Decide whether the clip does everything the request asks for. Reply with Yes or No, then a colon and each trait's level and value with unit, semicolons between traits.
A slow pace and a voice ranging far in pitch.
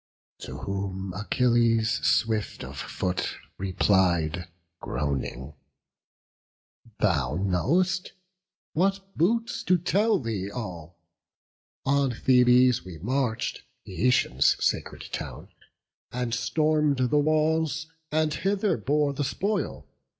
Yes: slow, 95 wpm; wide, 8.2 semitones